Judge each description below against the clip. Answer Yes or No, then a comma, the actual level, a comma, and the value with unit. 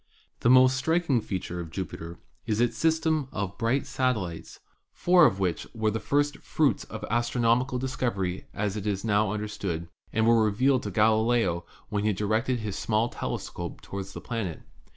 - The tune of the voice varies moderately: Yes, average, 4.4 semitones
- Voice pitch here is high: No, low, 110 Hz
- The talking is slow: No, average, 165 wpm